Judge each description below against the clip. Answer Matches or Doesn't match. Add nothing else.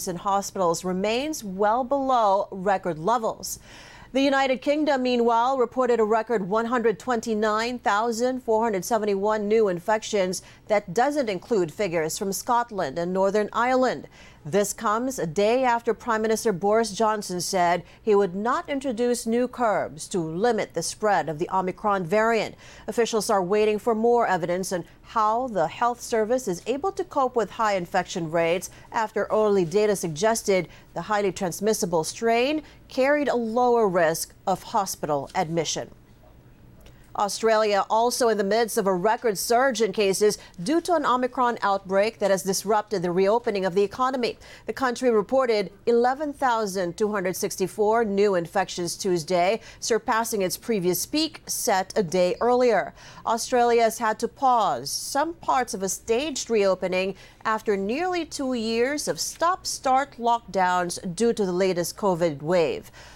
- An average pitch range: Matches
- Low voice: Doesn't match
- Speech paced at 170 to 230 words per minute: Doesn't match